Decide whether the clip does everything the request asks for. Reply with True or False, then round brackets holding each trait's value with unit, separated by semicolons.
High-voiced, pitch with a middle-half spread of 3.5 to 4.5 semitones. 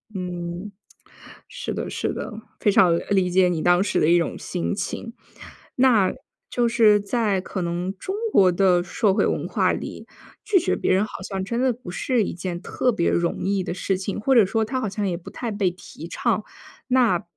True (195 Hz; 3.9 semitones)